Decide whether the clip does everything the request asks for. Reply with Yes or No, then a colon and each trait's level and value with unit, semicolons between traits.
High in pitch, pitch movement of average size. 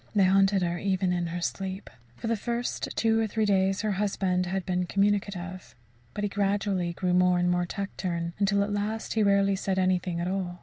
No: high, 195 Hz; narrow, 2.1 semitones